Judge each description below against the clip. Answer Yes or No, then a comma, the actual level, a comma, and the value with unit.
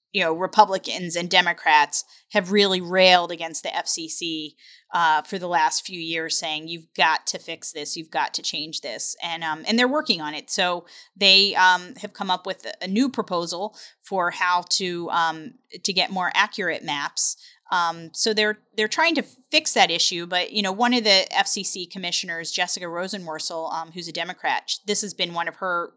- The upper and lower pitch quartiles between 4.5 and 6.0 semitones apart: No, average, 3.8 semitones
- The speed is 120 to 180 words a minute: No, average, 190 wpm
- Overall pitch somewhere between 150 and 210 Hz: Yes, medium, 185 Hz